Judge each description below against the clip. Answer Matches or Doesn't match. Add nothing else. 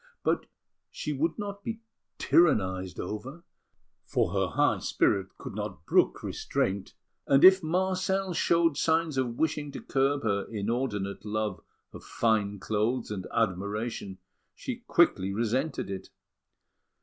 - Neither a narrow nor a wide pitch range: Doesn't match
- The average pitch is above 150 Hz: Doesn't match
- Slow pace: Matches